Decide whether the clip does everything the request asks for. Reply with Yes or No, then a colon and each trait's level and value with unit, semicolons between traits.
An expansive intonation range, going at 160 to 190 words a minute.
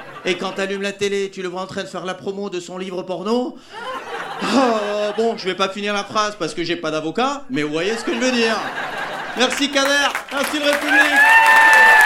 No: wide, 6.5 semitones; fast, 220 wpm